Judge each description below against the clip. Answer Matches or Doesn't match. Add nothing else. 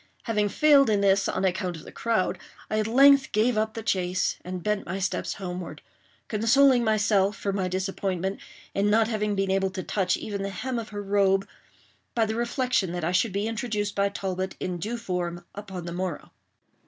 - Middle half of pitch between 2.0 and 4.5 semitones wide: Matches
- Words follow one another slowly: Doesn't match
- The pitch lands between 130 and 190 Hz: Doesn't match